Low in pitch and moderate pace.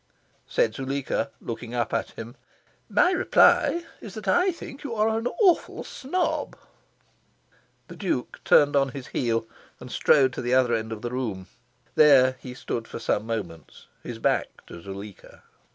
Yes: low, 130 Hz; average, 160 wpm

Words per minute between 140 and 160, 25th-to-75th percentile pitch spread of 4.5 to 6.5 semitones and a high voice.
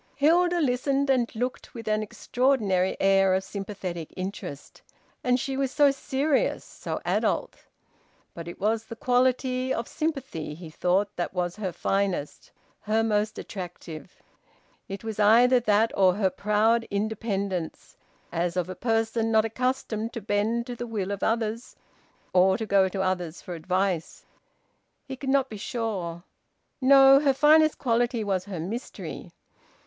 Yes: average, 150 wpm; average, 4.9 semitones; high, 215 Hz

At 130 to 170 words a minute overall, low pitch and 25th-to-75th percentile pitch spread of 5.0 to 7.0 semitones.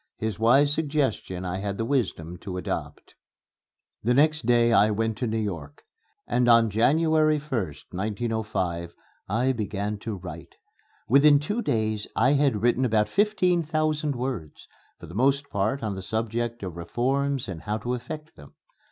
Yes: average, 160 wpm; low, 115 Hz; average, 5.3 semitones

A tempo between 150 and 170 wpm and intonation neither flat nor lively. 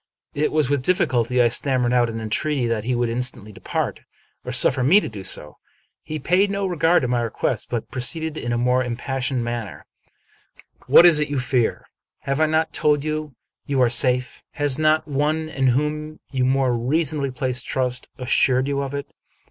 No: average, 195 wpm; average, 3.7 semitones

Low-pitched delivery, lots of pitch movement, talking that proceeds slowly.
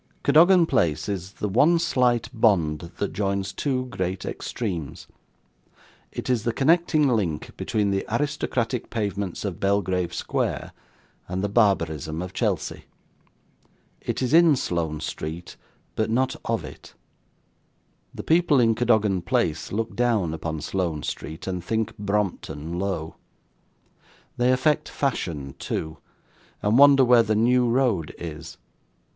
Yes: low, 105 Hz; wide, 6.3 semitones; slow, 130 wpm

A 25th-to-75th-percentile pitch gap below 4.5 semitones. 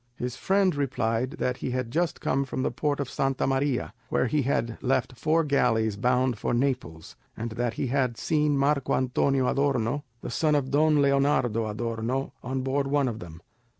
Yes: average, 2.9 semitones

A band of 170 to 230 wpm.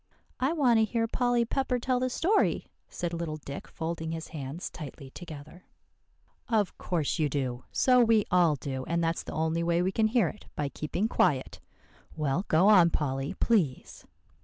Yes: average, 175 wpm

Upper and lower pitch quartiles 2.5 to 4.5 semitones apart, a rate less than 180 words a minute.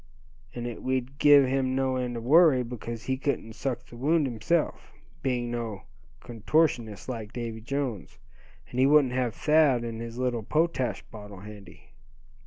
Yes: average, 2.9 semitones; average, 160 wpm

